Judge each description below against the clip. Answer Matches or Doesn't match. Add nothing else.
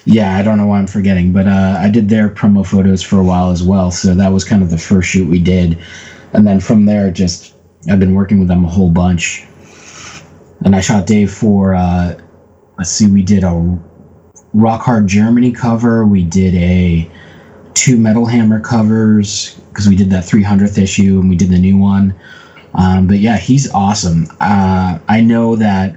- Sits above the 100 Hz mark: Doesn't match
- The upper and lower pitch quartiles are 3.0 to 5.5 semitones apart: Doesn't match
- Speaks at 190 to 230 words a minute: Matches